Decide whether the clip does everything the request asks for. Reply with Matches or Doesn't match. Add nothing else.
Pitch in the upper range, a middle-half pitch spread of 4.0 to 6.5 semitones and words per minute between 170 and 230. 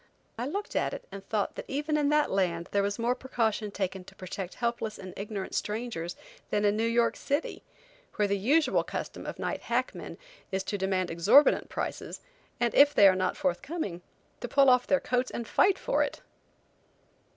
Matches